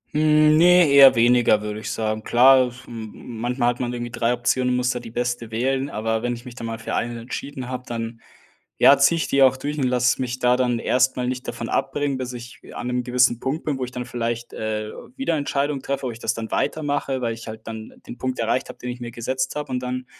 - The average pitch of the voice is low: Yes, low, 125 Hz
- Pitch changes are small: Yes, narrow, 2.1 semitones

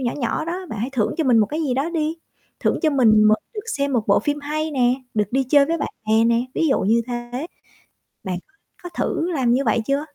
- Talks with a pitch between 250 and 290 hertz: Yes, very high, 265 Hz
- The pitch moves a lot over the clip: No, average, 4.8 semitones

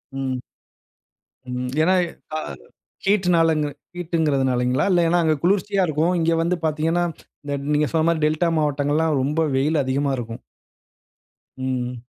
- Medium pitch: Yes, medium, 155 Hz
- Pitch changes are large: No, average, 3.8 semitones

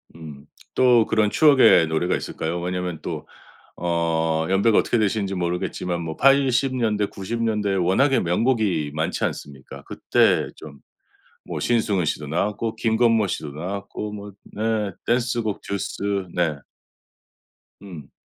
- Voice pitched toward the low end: Yes, low, 100 Hz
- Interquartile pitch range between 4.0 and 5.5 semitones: Yes, average, 4.9 semitones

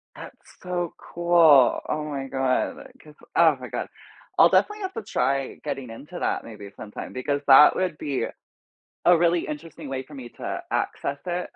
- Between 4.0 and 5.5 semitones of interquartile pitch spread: Yes, average, 4.4 semitones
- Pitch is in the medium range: Yes, medium, 145 Hz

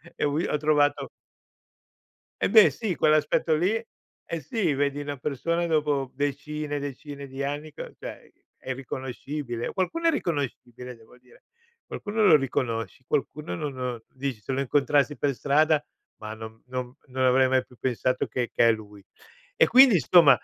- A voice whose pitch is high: No, medium, 140 Hz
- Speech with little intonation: No, average, 3.1 semitones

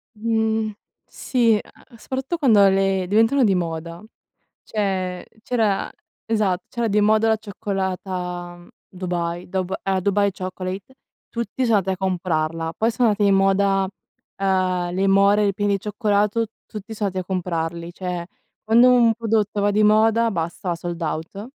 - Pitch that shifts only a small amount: No, average, 3.2 semitones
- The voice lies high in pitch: Yes, high, 195 Hz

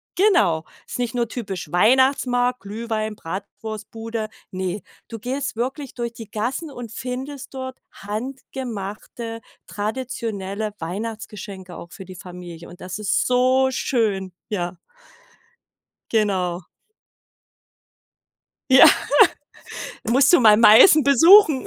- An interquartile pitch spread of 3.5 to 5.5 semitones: Yes, average, 4.5 semitones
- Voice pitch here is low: No, high, 225 Hz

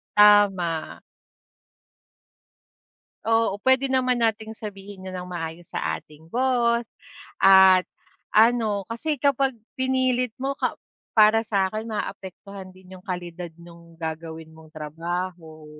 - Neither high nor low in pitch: No, high, 195 Hz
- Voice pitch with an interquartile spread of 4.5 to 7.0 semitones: Yes, average, 5.0 semitones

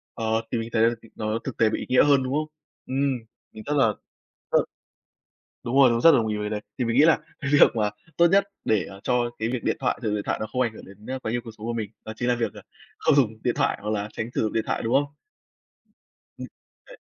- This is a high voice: No, low, 115 Hz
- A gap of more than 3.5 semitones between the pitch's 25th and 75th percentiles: No, average, 3.1 semitones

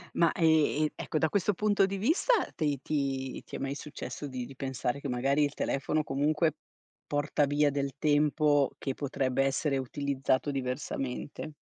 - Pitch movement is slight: Yes, narrow, 2.2 semitones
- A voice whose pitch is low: No, medium, 145 Hz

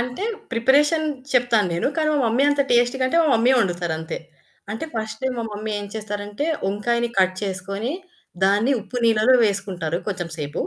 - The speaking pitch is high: Yes, high, 220 Hz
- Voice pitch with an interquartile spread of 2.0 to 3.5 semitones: No, average, 4.2 semitones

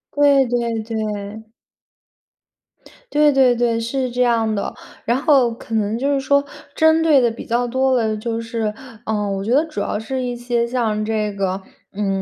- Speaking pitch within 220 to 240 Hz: Yes, high, 235 Hz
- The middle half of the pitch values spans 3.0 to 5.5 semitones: Yes, average, 3.3 semitones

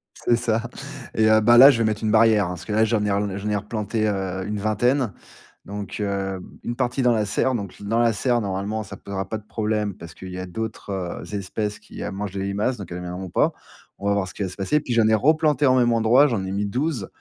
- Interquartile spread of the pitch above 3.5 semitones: No, average, 2.8 semitones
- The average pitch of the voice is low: Yes, low, 105 Hz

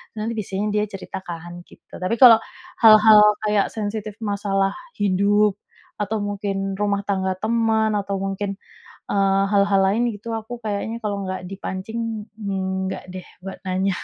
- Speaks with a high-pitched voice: Yes, high, 205 Hz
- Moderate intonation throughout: No, narrow, 1.8 semitones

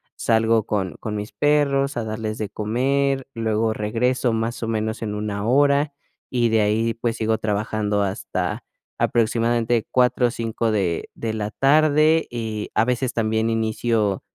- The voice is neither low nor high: No, low, 115 Hz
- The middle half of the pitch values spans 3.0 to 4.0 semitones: No, narrow, 2.4 semitones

